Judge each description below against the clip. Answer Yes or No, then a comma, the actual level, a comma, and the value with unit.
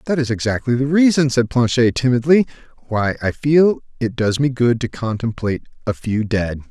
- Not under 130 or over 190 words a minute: Yes, average, 180 wpm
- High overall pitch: No, low, 125 Hz